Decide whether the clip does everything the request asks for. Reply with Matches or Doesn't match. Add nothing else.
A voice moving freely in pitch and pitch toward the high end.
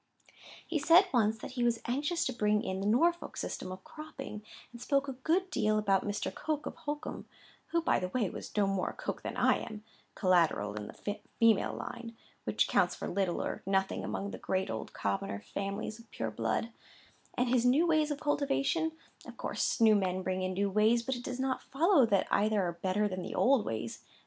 Matches